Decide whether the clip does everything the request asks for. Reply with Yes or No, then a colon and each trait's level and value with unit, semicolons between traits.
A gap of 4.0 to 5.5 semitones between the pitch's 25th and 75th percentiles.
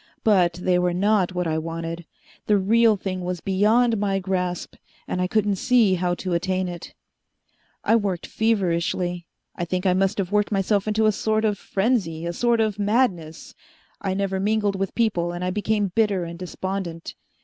No: average, 2.9 semitones